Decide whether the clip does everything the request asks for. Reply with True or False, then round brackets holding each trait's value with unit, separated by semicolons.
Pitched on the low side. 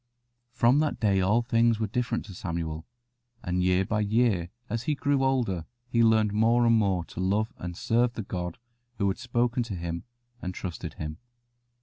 True (110 Hz)